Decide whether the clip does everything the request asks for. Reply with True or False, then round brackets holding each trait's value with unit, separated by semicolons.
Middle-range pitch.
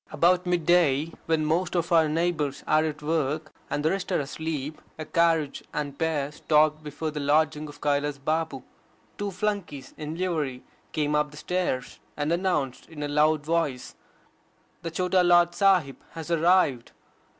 True (155 Hz)